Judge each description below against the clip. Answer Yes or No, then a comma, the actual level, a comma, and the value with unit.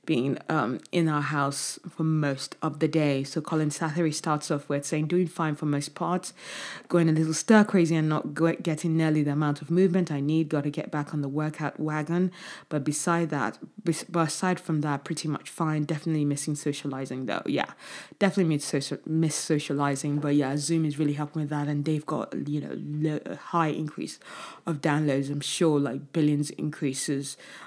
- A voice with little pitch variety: Yes, narrow, 1.9 semitones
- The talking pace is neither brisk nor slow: Yes, average, 190 wpm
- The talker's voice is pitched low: No, medium, 155 Hz